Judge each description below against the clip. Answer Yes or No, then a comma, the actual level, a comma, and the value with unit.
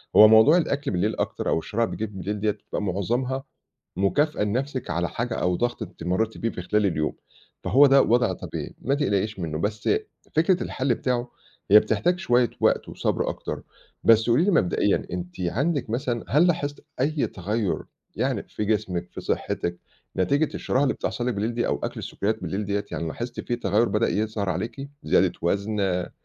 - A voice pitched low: Yes, low, 110 Hz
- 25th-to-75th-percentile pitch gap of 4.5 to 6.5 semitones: Yes, average, 4.8 semitones